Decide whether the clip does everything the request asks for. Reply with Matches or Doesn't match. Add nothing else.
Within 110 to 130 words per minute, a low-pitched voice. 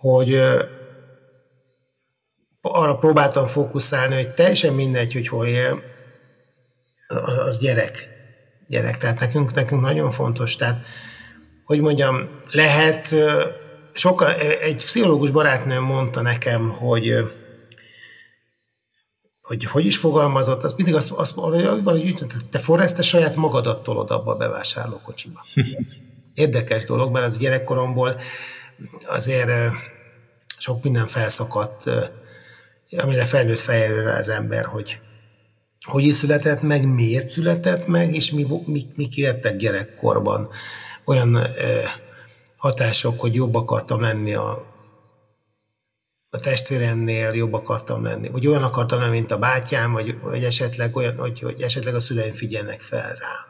Matches